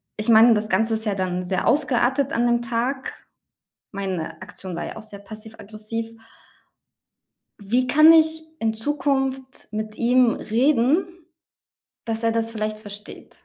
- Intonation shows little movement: No, average, 3.5 semitones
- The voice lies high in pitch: Yes, high, 225 Hz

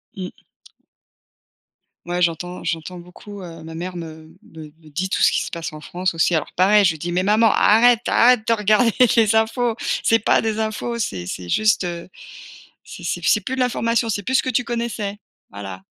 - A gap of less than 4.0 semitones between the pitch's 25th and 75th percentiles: No, average, 5.0 semitones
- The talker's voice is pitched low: No, high, 195 Hz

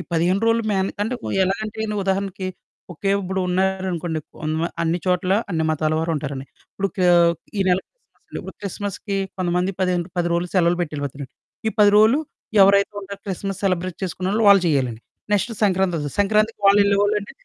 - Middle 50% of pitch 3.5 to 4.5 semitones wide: No, average, 2.8 semitones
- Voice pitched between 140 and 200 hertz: Yes, medium, 185 Hz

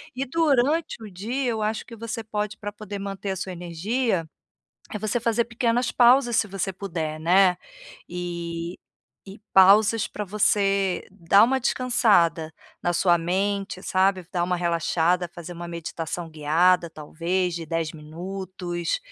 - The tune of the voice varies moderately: Yes, average, 4.0 semitones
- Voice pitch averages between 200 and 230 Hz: No, high, 190 Hz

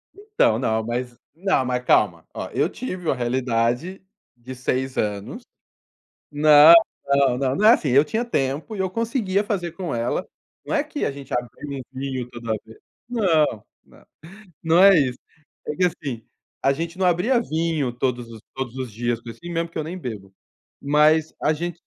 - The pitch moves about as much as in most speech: No, wide, 6.3 semitones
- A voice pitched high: No, medium, 145 Hz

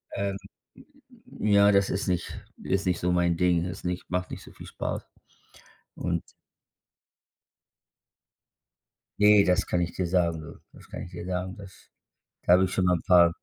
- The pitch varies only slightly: Yes, narrow, 1.6 semitones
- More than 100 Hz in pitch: No, very low, 90 Hz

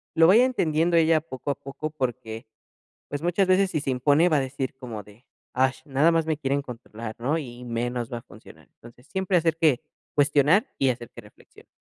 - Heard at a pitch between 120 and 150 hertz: Yes, medium, 140 Hz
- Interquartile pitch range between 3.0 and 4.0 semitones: No, average, 4.6 semitones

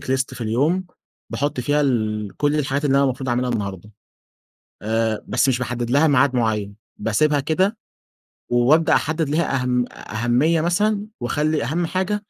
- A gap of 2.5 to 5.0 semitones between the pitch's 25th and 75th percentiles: Yes, average, 4.5 semitones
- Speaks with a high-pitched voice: No, low, 135 Hz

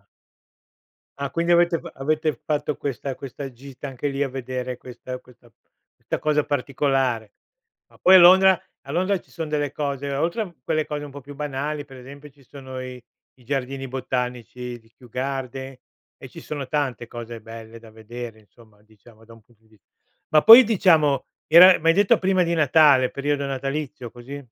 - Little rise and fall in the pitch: No, average, 3.3 semitones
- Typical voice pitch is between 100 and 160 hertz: Yes, low, 135 Hz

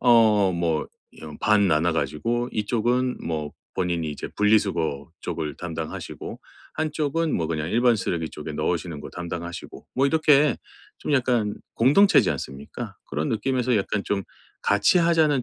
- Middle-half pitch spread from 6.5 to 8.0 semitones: Yes, wide, 7.4 semitones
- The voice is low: Yes, low, 100 Hz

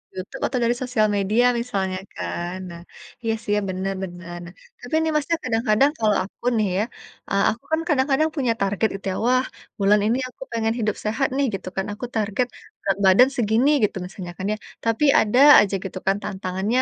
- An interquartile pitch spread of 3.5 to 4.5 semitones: Yes, average, 4.2 semitones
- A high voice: Yes, high, 215 Hz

